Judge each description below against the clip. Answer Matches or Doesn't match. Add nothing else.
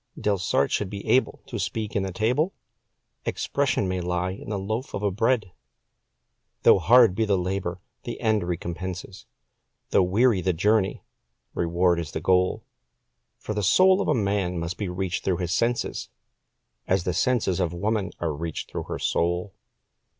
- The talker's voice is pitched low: Matches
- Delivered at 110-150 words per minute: Doesn't match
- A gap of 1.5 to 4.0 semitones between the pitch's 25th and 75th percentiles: Matches